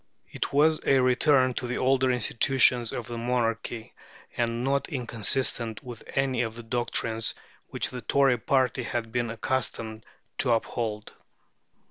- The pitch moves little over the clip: Yes, narrow, 2.3 semitones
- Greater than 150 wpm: No, average, 140 wpm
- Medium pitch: No, low, 120 Hz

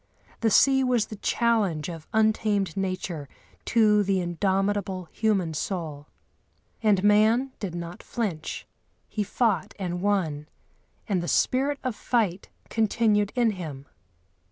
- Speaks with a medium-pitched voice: No, high, 200 Hz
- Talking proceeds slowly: Yes, slow, 125 wpm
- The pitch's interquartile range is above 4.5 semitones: No, average, 4.0 semitones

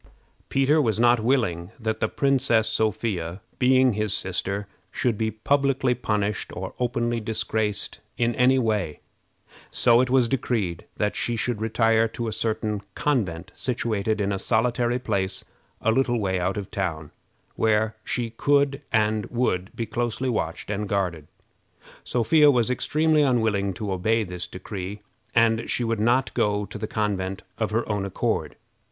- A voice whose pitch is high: No, low, 110 Hz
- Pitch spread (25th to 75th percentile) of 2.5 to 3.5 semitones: Yes, average, 3.2 semitones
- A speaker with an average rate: Yes, average, 150 wpm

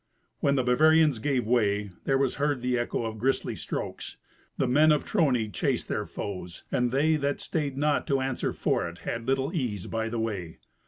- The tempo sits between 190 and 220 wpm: Yes, average, 195 wpm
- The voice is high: No, low, 130 Hz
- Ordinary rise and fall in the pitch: Yes, average, 4.1 semitones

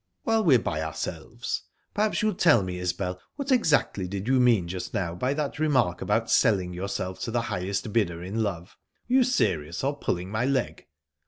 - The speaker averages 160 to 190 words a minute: Yes, average, 185 wpm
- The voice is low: Yes, low, 105 Hz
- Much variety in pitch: Yes, wide, 7.4 semitones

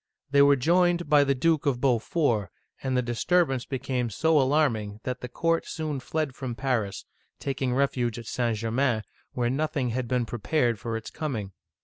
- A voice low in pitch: Yes, low, 130 Hz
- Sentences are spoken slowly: No, average, 180 wpm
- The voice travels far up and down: No, average, 3.8 semitones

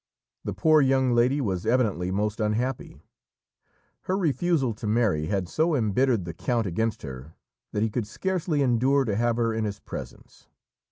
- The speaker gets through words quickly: No, average, 165 wpm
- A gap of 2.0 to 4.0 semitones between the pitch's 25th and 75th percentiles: No, average, 4.4 semitones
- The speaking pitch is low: Yes, low, 115 Hz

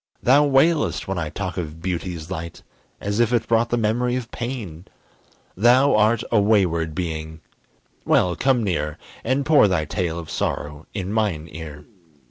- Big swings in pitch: Yes, wide, 6.4 semitones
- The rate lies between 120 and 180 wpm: Yes, average, 160 wpm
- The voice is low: Yes, very low, 95 Hz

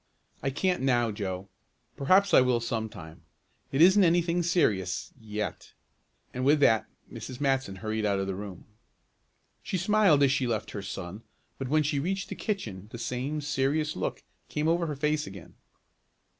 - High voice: No, low, 135 Hz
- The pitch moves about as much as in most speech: No, wide, 6.6 semitones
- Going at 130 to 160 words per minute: No, average, 170 wpm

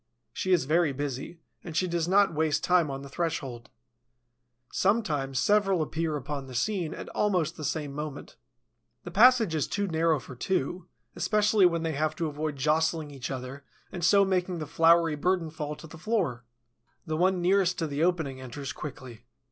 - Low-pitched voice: No, medium, 160 Hz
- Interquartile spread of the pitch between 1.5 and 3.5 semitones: No, average, 4.0 semitones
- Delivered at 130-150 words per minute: No, average, 180 wpm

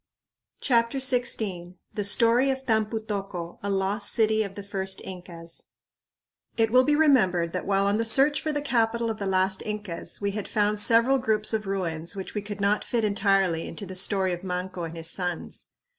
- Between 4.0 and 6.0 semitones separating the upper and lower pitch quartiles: No, average, 3.4 semitones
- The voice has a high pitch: Yes, high, 205 Hz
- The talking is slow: No, average, 190 wpm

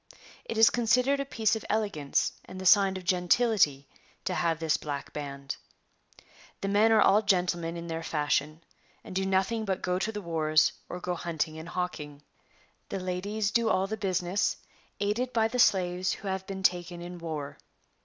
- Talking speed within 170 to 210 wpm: Yes, average, 180 wpm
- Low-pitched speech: No, medium, 185 Hz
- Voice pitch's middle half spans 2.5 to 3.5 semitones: No, average, 4.1 semitones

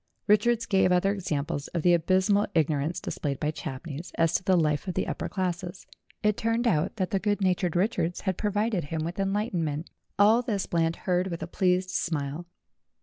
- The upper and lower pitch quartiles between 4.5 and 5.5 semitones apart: No, average, 3.5 semitones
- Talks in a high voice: No, medium, 180 Hz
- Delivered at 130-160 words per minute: No, average, 190 wpm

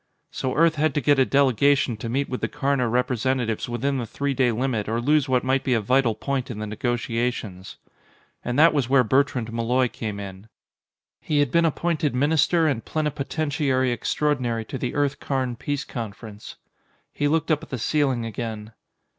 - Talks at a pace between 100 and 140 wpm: No, average, 180 wpm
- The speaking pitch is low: Yes, low, 130 Hz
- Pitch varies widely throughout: No, average, 3.7 semitones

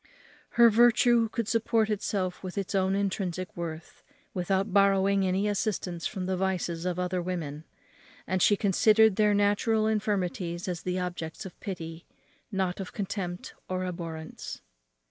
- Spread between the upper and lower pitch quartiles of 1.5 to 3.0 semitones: Yes, narrow, 2.5 semitones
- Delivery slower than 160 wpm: Yes, average, 145 wpm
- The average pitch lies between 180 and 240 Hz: Yes, high, 190 Hz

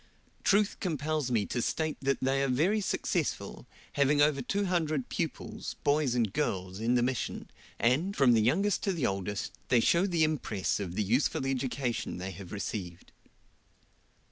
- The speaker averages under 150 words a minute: No, average, 165 wpm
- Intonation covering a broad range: Yes, wide, 6.0 semitones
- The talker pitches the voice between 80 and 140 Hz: Yes, low, 135 Hz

